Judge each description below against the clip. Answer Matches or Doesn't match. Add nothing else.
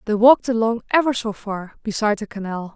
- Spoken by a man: Doesn't match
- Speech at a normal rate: Matches